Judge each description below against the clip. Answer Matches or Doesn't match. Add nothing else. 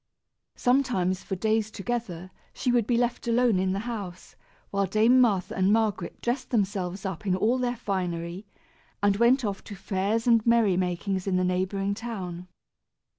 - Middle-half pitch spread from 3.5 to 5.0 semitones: Matches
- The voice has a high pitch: Matches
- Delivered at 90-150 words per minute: Doesn't match